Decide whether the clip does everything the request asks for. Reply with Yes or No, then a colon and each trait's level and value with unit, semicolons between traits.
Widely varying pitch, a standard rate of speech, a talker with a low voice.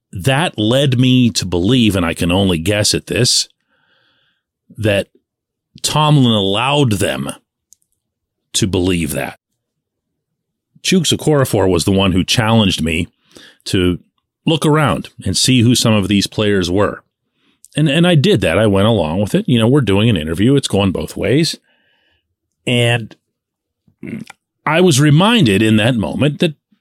Yes: wide, 6.2 semitones; average, 150 wpm; low, 110 Hz